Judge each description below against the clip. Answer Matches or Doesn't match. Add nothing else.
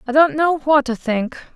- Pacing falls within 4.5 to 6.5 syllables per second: Matches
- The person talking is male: Doesn't match